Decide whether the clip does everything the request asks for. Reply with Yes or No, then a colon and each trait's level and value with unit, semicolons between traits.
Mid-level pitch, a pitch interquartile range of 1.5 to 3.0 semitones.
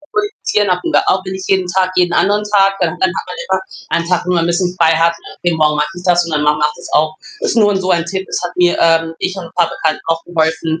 Yes: medium, 175 Hz; narrow, 2.4 semitones